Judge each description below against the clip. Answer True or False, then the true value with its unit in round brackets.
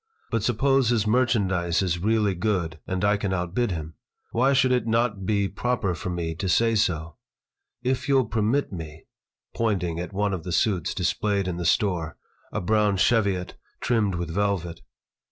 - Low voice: True (100 Hz)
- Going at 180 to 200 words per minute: False (170 wpm)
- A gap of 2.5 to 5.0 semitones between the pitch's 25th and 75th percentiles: True (4.5 semitones)